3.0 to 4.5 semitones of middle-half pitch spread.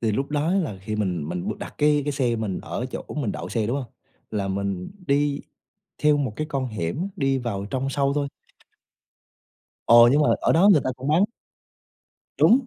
No: wide, 5.4 semitones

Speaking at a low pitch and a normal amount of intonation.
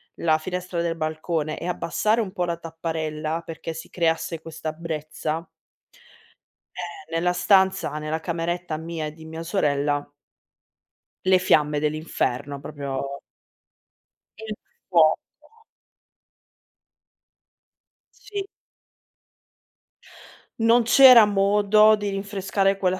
No: medium, 165 Hz; average, 3.7 semitones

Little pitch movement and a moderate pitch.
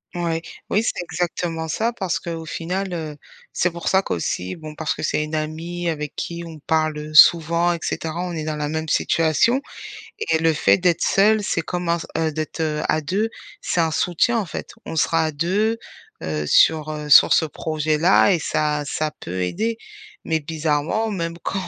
Yes: narrow, 2.3 semitones; medium, 160 Hz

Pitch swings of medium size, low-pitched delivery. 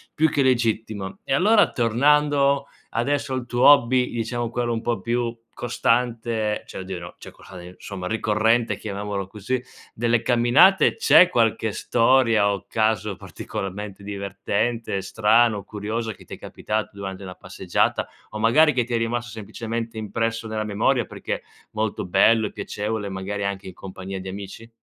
Yes: average, 3.0 semitones; low, 110 Hz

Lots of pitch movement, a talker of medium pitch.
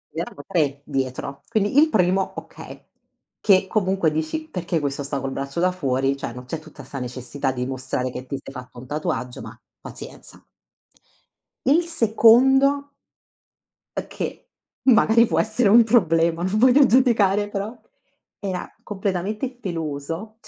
Yes: wide, 7.9 semitones; medium, 180 Hz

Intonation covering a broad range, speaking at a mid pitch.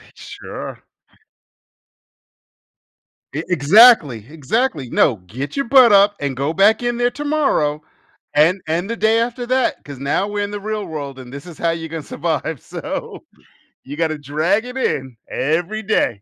Yes: wide, 7.3 semitones; medium, 170 Hz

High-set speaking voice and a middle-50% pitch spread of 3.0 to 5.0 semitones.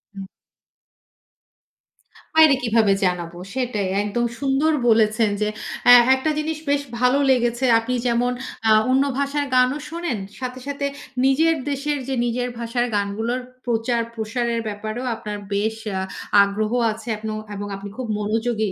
Yes: high, 235 Hz; average, 3.5 semitones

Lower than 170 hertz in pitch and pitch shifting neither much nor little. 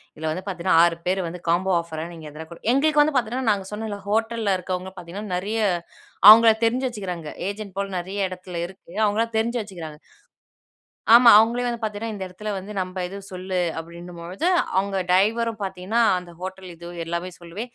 No: high, 190 Hz; average, 3.7 semitones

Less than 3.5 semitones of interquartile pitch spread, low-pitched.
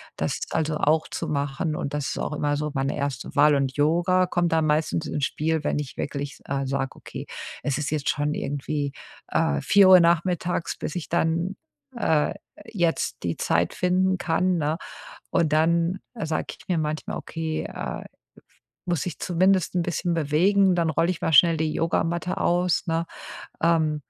No: average, 2.8 semitones; medium, 160 Hz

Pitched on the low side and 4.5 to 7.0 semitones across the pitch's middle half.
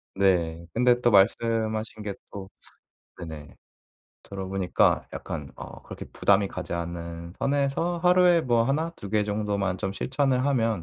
Yes: low, 105 Hz; average, 5.3 semitones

